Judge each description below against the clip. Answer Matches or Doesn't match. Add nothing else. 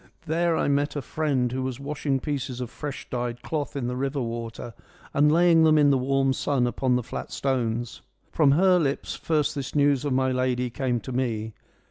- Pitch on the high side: Doesn't match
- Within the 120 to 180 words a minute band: Doesn't match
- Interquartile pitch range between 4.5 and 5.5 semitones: Doesn't match